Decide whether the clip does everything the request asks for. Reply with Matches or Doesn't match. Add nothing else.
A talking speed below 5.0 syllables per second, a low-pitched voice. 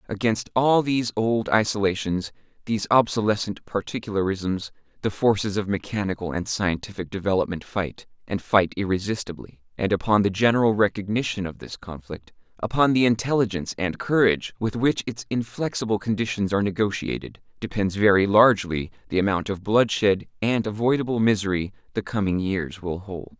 Doesn't match